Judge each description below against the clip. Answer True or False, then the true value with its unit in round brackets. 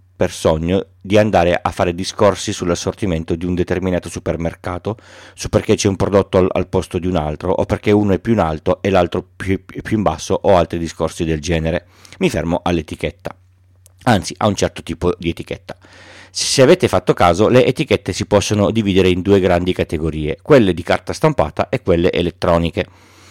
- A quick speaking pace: True (185 wpm)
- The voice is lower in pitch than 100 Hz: True (90 Hz)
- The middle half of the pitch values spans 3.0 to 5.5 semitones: False (2.6 semitones)